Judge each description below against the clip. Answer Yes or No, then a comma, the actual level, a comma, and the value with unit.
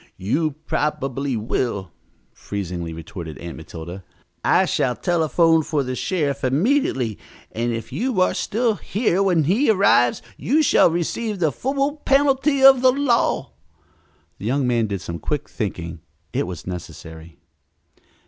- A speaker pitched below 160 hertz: Yes, medium, 140 Hz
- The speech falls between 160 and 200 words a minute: No, average, 140 wpm